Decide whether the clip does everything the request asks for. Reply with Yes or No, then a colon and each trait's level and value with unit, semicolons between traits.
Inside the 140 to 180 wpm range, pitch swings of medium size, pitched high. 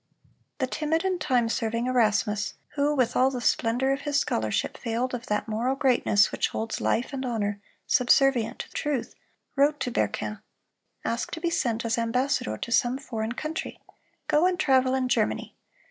Yes: average, 170 wpm; average, 3.2 semitones; very high, 250 Hz